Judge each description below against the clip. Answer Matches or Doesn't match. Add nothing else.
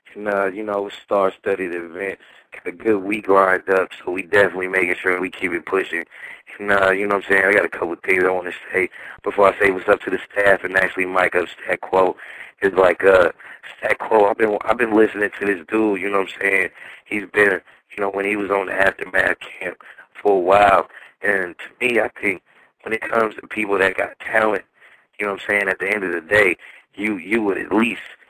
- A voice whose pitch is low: Matches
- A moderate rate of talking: Doesn't match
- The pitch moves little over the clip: Matches